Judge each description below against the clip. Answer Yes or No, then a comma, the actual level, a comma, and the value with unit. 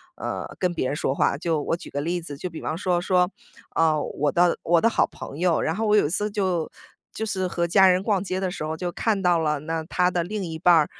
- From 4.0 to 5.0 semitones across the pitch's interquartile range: No, average, 2.7 semitones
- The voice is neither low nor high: Yes, medium, 175 Hz